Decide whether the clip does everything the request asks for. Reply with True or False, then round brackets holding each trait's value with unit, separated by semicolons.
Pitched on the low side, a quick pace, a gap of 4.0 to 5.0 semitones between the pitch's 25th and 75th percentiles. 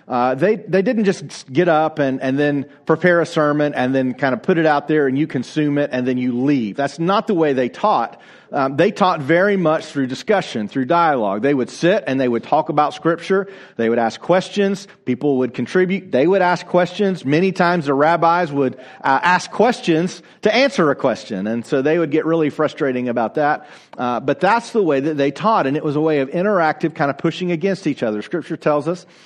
False (155 Hz; 225 wpm; 4.7 semitones)